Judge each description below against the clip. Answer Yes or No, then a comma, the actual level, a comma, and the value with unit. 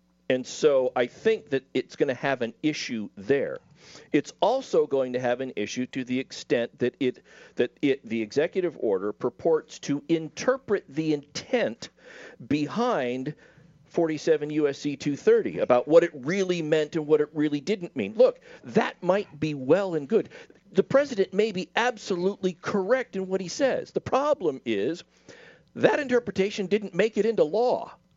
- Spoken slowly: No, average, 160 wpm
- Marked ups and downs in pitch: Yes, wide, 7.1 semitones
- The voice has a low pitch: No, medium, 175 Hz